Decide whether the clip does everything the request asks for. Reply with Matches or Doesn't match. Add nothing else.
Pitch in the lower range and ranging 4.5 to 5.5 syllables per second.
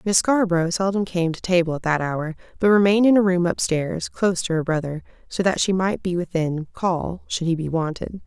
Doesn't match